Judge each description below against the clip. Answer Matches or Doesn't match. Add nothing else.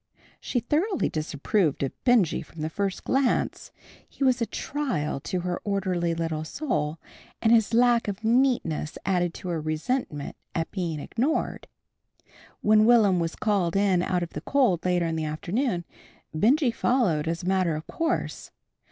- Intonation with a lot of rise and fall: Matches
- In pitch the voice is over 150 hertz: Matches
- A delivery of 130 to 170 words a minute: Matches